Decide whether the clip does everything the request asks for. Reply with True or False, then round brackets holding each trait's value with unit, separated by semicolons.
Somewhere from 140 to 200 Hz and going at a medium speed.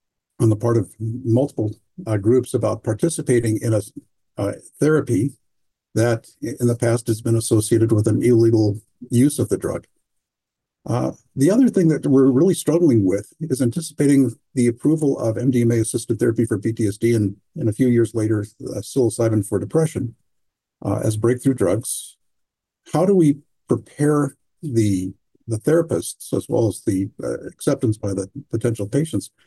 False (120 Hz; 155 wpm)